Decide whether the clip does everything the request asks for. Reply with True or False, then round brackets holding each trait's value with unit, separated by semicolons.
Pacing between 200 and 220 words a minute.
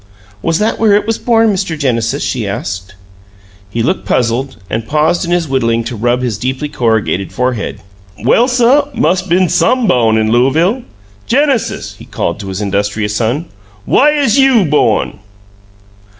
False (160 wpm)